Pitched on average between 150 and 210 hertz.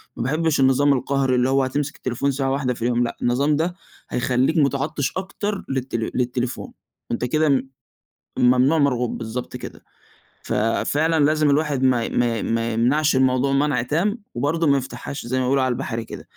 No: low, 135 Hz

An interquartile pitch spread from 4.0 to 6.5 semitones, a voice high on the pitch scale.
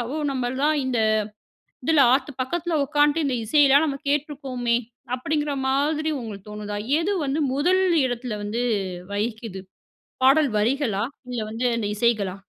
Yes: average, 4.5 semitones; very high, 265 Hz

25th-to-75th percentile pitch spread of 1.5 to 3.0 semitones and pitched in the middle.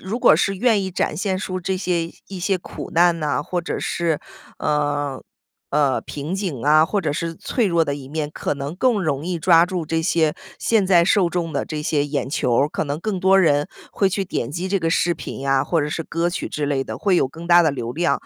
No: average, 4.0 semitones; medium, 165 Hz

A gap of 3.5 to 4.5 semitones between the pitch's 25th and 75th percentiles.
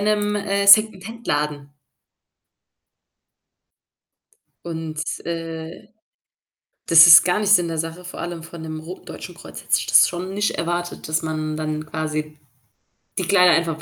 No: average, 3.0 semitones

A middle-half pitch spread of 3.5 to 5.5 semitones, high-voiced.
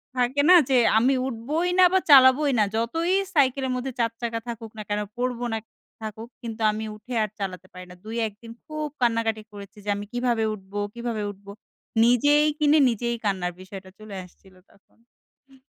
Yes: average, 3.8 semitones; high, 230 Hz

